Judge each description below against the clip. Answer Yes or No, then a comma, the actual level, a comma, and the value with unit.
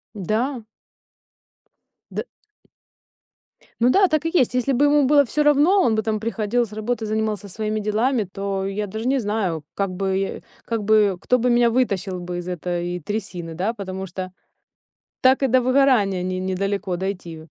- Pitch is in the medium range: No, high, 215 Hz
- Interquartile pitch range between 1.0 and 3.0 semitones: No, average, 4.6 semitones